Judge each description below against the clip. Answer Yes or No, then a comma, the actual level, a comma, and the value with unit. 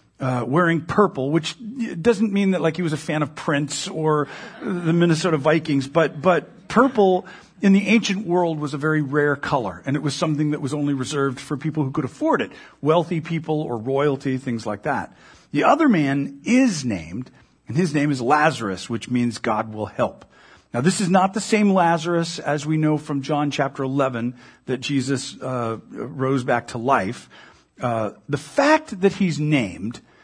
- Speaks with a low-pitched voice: No, medium, 155 Hz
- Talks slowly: No, average, 185 wpm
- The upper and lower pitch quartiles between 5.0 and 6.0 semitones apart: No, average, 4.6 semitones